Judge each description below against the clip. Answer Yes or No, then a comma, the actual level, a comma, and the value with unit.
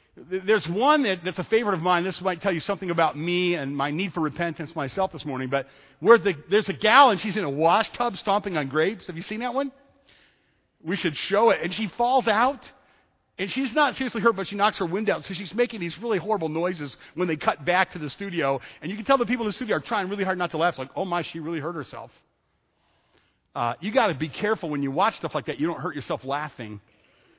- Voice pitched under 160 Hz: No, medium, 185 Hz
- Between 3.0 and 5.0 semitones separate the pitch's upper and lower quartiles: No, wide, 5.4 semitones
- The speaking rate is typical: No, fast, 255 wpm